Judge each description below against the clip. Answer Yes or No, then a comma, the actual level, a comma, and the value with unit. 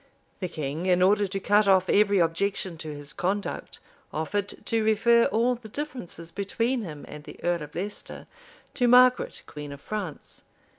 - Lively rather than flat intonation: No, average, 4.7 semitones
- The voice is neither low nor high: No, high, 195 Hz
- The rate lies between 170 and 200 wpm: Yes, average, 175 wpm